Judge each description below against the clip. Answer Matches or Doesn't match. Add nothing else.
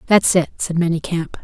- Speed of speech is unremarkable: Matches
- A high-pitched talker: Doesn't match